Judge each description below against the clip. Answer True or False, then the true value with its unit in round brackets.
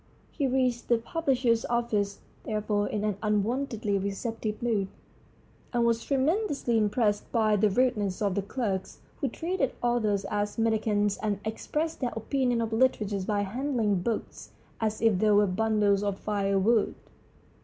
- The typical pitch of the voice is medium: False (220 Hz)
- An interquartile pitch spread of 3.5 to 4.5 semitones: False (2.8 semitones)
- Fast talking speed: False (145 wpm)